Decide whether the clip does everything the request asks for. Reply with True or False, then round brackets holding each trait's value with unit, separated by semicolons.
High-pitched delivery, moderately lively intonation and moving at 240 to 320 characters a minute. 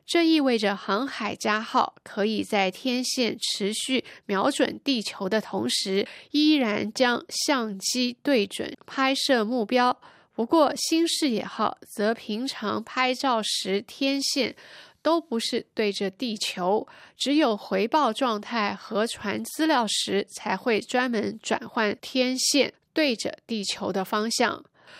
False (235 Hz; 3.9 semitones; 190 characters per minute)